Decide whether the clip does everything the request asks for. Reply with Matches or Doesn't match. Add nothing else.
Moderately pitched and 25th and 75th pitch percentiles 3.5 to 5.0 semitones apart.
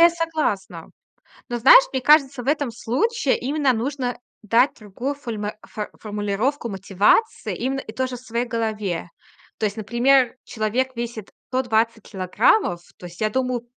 Doesn't match